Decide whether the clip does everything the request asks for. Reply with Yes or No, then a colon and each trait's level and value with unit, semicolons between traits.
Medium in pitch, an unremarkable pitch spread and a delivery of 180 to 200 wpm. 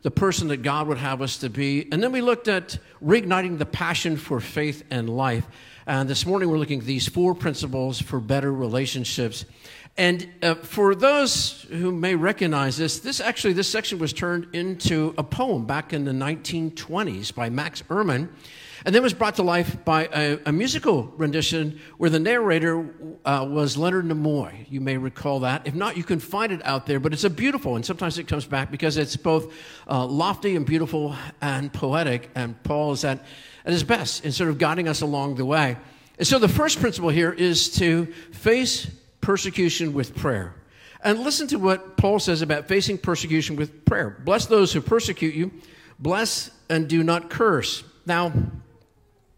Yes: medium, 155 Hz; average, 4.3 semitones; average, 190 wpm